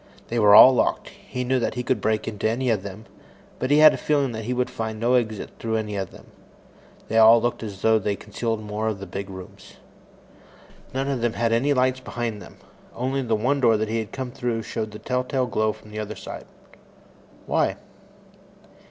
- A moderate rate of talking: No, fast, 215 wpm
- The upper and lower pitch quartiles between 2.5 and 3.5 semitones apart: Yes, average, 2.8 semitones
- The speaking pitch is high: No, low, 115 Hz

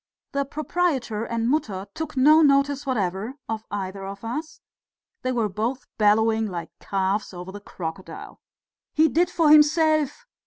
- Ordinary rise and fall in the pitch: No, wide, 6.8 semitones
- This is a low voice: No, high, 235 Hz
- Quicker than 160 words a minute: No, average, 145 wpm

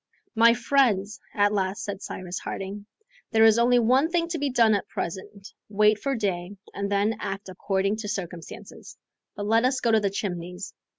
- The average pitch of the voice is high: Yes, high, 205 Hz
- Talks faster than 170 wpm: Yes, average, 180 wpm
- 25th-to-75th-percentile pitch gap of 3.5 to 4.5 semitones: No, average, 2.9 semitones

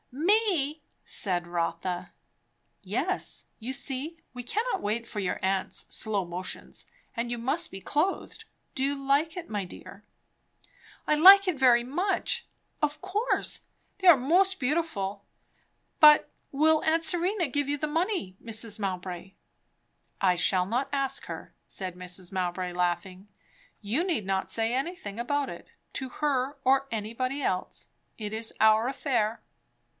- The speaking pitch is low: No, very high, 250 Hz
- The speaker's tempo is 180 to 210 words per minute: No, average, 140 wpm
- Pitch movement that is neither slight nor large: No, wide, 7.6 semitones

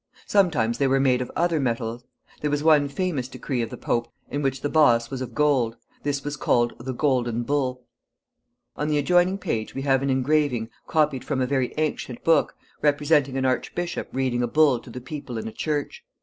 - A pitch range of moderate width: Yes, average, 3.2 semitones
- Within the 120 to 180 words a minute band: No, average, 200 wpm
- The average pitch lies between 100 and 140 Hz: Yes, low, 135 Hz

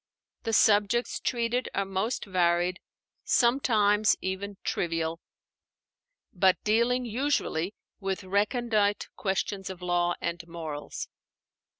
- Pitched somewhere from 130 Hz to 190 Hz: No, high, 200 Hz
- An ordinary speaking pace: No, slow, 95 wpm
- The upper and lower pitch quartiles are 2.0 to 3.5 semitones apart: No, average, 4.2 semitones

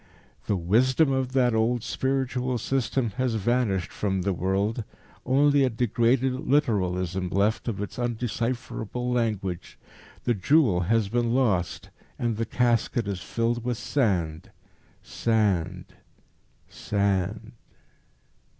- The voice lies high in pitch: No, low, 115 Hz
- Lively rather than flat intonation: No, average, 4.1 semitones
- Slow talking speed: Yes, slow, 115 wpm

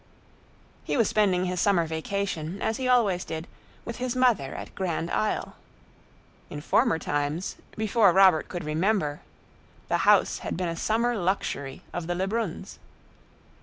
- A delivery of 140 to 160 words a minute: Yes, average, 145 wpm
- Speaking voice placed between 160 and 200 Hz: Yes, medium, 185 Hz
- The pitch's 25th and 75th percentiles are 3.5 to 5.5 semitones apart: Yes, average, 4.8 semitones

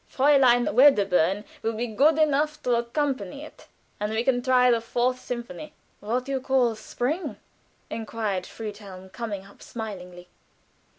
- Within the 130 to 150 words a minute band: Yes, slow, 135 wpm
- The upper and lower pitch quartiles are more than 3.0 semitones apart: Yes, average, 4.2 semitones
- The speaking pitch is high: Yes, high, 240 Hz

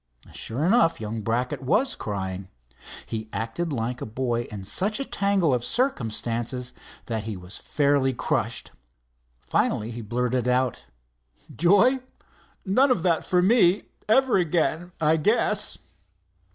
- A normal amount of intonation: No, wide, 8.4 semitones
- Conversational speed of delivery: No, slow, 130 wpm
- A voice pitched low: Yes, low, 130 Hz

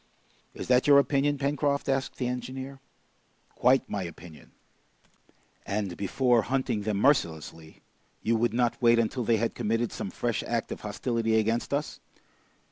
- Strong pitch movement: No, average, 3.8 semitones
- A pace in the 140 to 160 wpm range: Yes, average, 145 wpm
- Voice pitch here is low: Yes, low, 120 Hz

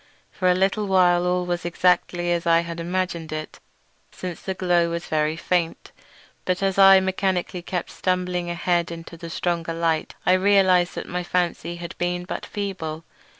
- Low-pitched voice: No, medium, 175 Hz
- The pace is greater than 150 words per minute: Yes, average, 175 wpm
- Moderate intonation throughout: No, narrow, 1.5 semitones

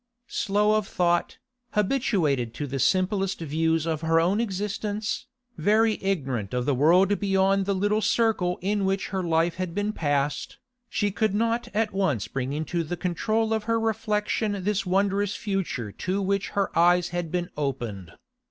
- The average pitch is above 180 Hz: Yes, high, 190 Hz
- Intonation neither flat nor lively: Yes, average, 4.1 semitones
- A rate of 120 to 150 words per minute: No, average, 160 wpm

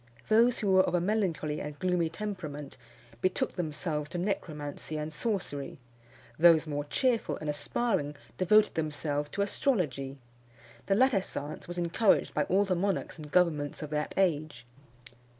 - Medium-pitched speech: Yes, medium, 170 Hz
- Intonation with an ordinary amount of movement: Yes, average, 4.7 semitones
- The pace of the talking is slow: No, average, 150 wpm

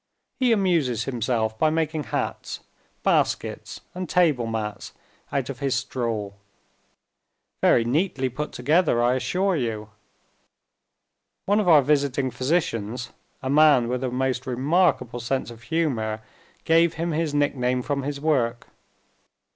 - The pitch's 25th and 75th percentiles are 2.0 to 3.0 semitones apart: No, average, 4.7 semitones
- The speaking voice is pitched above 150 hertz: No, low, 135 Hz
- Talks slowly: Yes, slow, 130 wpm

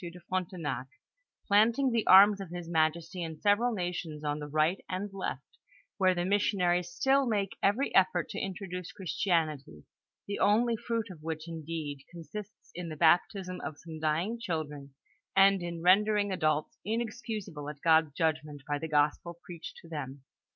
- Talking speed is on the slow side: No, average, 165 wpm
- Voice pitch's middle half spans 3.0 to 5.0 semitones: Yes, average, 4.3 semitones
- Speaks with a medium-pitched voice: Yes, medium, 175 Hz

